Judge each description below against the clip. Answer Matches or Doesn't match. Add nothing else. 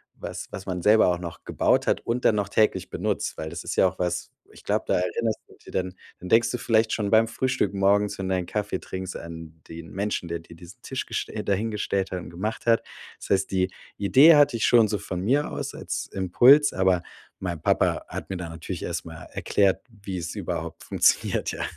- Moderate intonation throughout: Matches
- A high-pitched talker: Doesn't match